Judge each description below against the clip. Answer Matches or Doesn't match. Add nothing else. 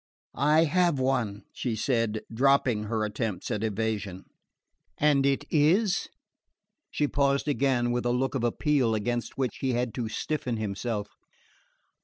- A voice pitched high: Doesn't match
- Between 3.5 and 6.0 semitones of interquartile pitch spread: Matches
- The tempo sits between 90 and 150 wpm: Matches